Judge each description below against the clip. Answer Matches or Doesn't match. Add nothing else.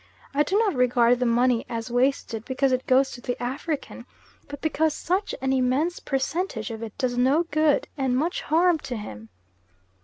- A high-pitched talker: Matches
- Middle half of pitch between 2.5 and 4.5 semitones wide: Matches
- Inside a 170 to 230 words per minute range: Matches